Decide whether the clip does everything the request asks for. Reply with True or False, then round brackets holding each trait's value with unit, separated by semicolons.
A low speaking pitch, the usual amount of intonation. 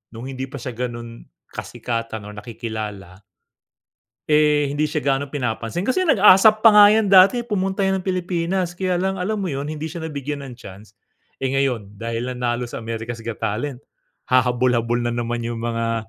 False (130 Hz; 7.3 semitones)